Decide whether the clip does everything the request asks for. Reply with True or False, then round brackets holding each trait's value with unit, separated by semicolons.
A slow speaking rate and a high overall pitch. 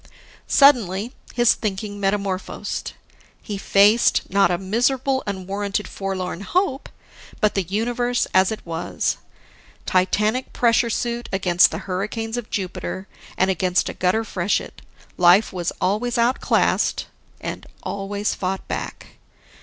True (120 wpm; 200 Hz)